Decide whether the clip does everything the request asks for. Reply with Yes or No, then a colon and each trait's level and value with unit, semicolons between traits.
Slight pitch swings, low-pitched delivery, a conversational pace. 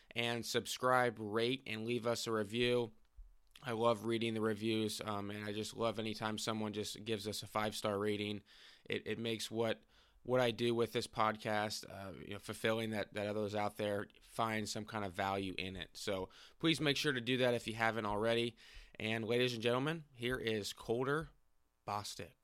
Yes: narrow, 2.1 semitones; low, 110 Hz; average, 195 wpm